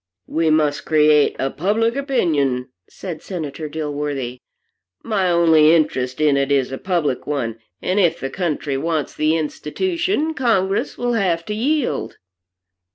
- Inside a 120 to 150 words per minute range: Yes, average, 140 wpm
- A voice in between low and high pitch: Yes, medium, 160 Hz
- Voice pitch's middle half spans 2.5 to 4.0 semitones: No, average, 5.2 semitones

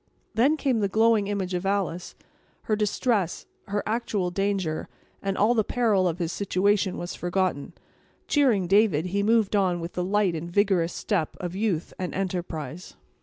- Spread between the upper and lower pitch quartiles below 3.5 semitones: Yes, average, 2.9 semitones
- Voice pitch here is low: No, high, 195 Hz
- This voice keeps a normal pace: Yes, average, 165 wpm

